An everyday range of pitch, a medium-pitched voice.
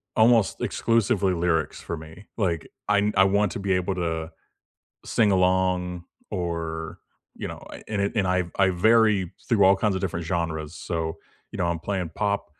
No: average, 3.1 semitones; very low, 90 Hz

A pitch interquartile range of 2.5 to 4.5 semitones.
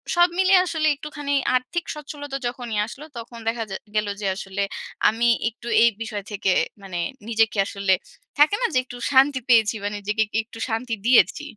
No: average, 5.2 semitones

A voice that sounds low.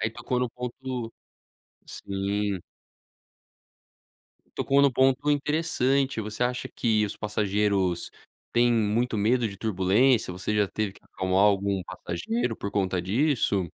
Yes: low, 110 Hz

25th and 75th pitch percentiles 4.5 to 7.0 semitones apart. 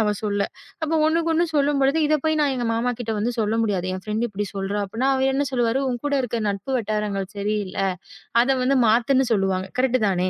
Yes: average, 4.9 semitones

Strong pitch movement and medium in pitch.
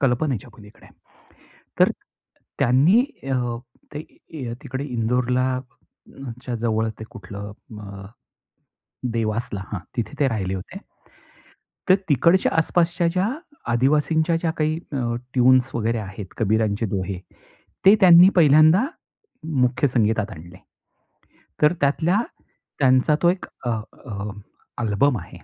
No: wide, 5.7 semitones; low, 125 Hz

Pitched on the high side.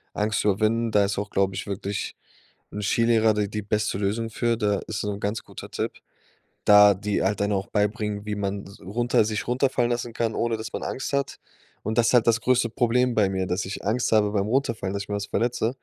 No: low, 105 Hz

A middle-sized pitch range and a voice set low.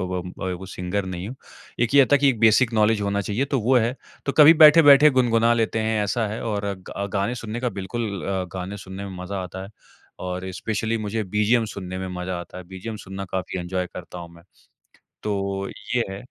Yes: average, 3.7 semitones; low, 105 Hz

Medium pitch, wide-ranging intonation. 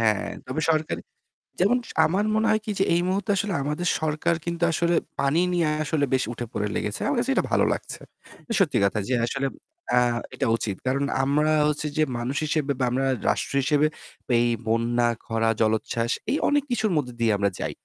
Yes: medium, 145 Hz; wide, 6.2 semitones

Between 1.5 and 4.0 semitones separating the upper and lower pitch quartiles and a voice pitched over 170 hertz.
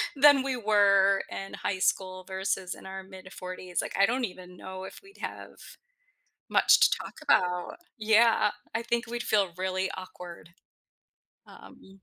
Yes: average, 2.9 semitones; high, 190 Hz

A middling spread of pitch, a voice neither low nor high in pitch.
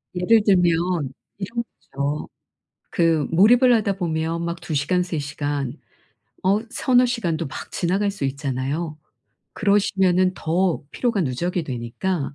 Yes: average, 4.7 semitones; medium, 175 Hz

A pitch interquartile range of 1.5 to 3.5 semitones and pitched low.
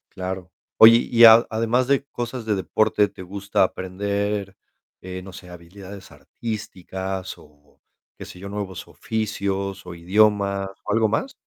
Yes: average, 2.8 semitones; low, 100 Hz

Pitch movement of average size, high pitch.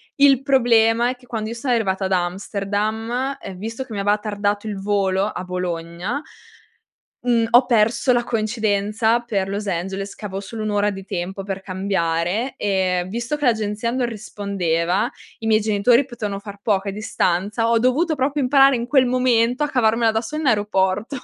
Yes: average, 3.6 semitones; high, 215 Hz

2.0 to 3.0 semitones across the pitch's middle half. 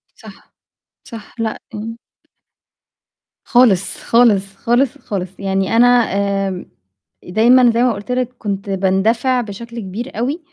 No: average, 3.6 semitones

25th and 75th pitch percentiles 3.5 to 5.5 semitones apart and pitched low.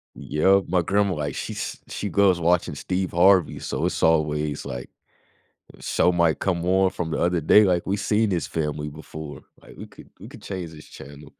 Yes: average, 3.8 semitones; very low, 85 Hz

